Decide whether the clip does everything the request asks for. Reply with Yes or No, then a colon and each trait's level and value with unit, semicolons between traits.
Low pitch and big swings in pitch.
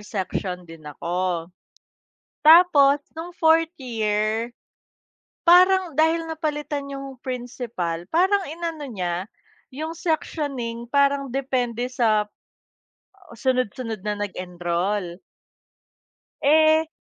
No: very high, 255 Hz; wide, 7.1 semitones